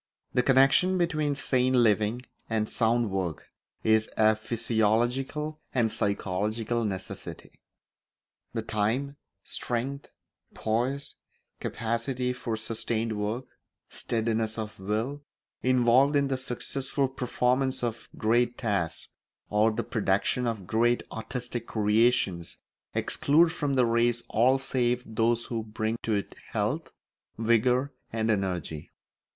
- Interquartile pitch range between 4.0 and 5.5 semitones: No, average, 2.8 semitones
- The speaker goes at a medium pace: No, slow, 110 wpm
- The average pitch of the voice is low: Yes, low, 115 Hz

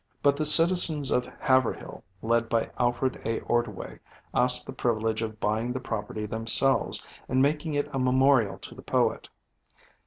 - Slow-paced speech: No, average, 155 wpm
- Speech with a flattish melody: No, average, 3.2 semitones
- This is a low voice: Yes, low, 125 Hz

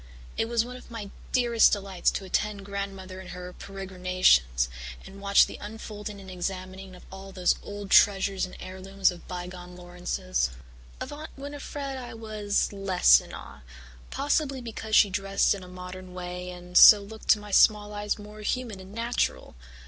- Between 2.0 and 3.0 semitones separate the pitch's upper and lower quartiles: Yes, narrow, 2.6 semitones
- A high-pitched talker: Yes, high, 195 Hz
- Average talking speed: Yes, average, 170 wpm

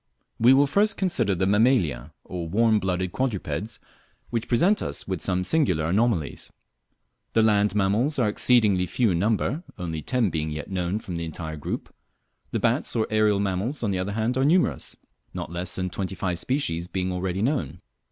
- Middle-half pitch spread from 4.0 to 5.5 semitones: Yes, average, 4.7 semitones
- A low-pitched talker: Yes, low, 100 Hz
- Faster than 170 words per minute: Yes, average, 180 wpm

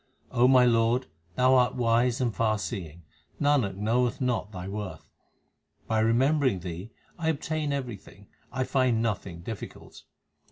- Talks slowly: Yes, slow, 130 wpm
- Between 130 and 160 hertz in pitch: No, low, 115 Hz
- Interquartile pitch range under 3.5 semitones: No, average, 3.9 semitones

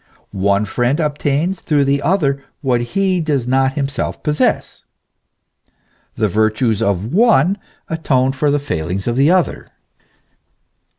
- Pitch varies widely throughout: No, average, 4.6 semitones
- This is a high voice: No, low, 135 Hz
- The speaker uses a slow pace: Yes, slow, 130 wpm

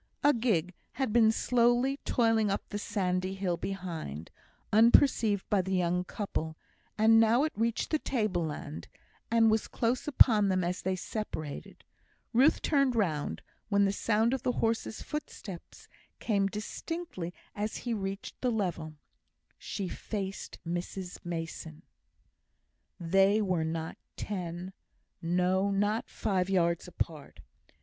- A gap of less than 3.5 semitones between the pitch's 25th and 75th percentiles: No, average, 4.1 semitones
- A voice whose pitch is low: No, high, 200 Hz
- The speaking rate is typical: No, slow, 130 wpm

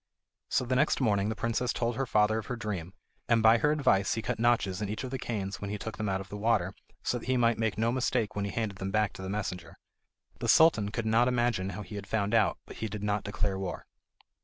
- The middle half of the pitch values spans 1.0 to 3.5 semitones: Yes, average, 2.7 semitones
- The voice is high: No, low, 110 Hz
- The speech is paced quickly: Yes, fast, 260 wpm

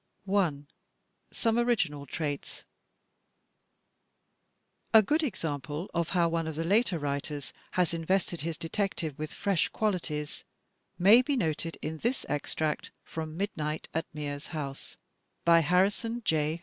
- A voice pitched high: No, medium, 165 Hz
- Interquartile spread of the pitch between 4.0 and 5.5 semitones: Yes, average, 4.5 semitones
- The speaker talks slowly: Yes, slow, 125 wpm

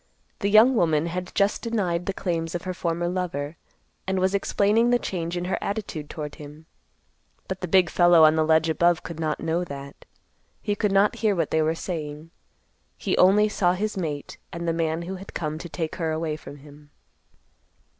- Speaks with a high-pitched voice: No, medium, 170 Hz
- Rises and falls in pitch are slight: No, average, 3.2 semitones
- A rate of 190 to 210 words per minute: Yes, average, 195 wpm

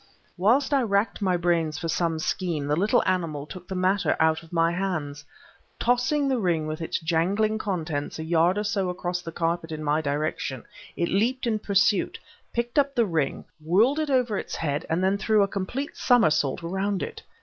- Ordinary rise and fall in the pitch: Yes, average, 4.7 semitones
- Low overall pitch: No, medium, 180 Hz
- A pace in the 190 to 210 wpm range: Yes, average, 195 wpm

